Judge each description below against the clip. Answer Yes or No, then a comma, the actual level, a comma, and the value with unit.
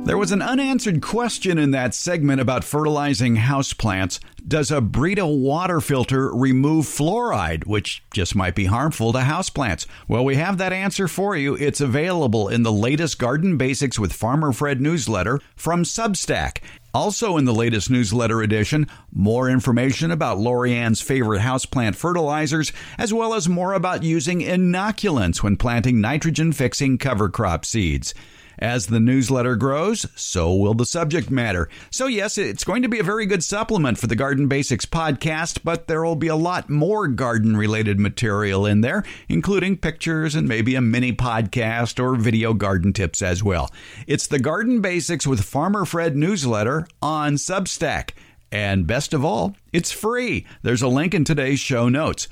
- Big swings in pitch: Yes, wide, 6.7 semitones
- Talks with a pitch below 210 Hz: Yes, low, 135 Hz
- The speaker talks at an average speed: Yes, average, 165 wpm